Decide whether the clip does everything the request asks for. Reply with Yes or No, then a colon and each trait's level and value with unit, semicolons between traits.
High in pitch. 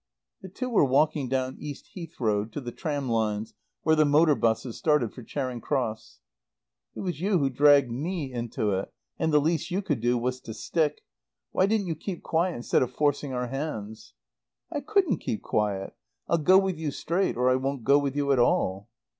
No: medium, 140 Hz